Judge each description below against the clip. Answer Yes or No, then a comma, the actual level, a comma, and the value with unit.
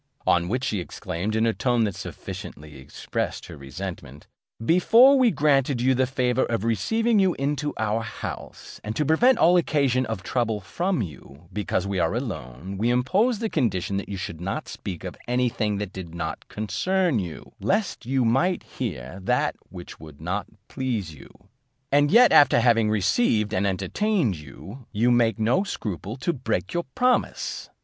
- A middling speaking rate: Yes, average, 170 wpm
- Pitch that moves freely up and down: Yes, wide, 7.2 semitones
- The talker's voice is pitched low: Yes, low, 115 Hz